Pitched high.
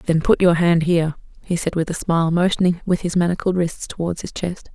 No: medium, 170 Hz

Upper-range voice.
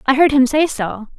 Yes: very high, 270 Hz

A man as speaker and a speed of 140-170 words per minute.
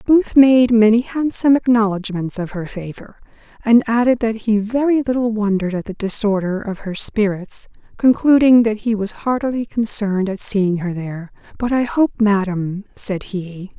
No: female; average, 160 wpm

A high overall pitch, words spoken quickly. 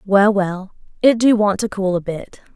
Yes: high, 200 Hz; fast, 210 wpm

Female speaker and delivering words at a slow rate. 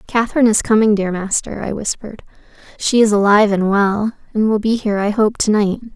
No: female; average, 200 wpm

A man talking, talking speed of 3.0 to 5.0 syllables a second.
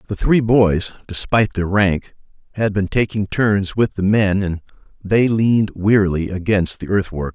Yes: male; 4.5 syllables/s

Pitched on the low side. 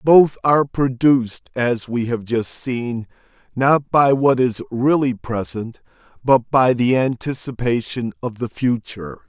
Yes: low, 125 Hz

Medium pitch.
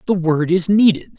Yes: medium, 180 Hz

